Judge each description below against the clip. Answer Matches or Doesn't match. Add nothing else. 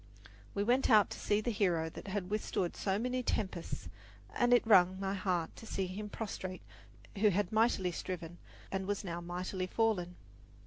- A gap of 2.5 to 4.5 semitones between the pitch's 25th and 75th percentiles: Matches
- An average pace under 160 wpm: Doesn't match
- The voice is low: Doesn't match